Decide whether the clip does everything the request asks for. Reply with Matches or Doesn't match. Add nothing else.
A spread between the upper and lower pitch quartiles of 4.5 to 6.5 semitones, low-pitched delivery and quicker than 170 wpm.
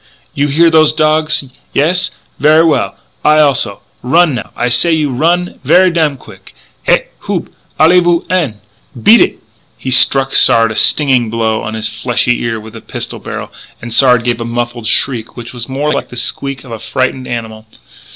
Matches